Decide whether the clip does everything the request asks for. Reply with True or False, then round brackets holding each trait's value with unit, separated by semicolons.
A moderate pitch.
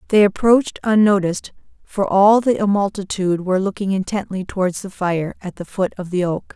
False (195 Hz)